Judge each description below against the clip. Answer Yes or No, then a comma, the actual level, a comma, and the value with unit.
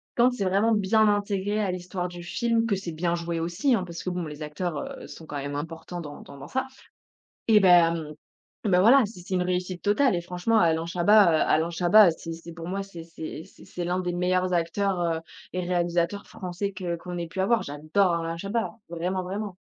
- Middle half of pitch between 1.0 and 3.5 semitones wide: Yes, average, 2.9 semitones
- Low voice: No, medium, 180 Hz